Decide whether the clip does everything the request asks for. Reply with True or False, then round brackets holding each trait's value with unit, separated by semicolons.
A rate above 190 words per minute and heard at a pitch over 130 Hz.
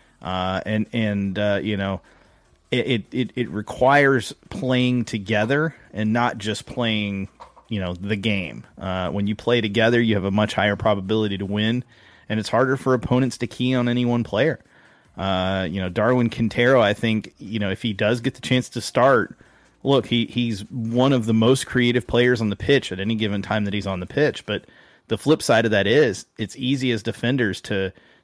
False (200 wpm; 110 Hz)